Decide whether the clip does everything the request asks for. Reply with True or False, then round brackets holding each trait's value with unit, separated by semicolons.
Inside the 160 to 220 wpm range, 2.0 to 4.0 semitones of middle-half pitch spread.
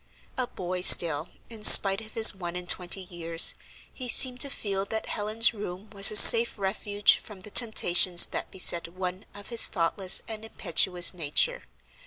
True (170 wpm; 3.6 semitones)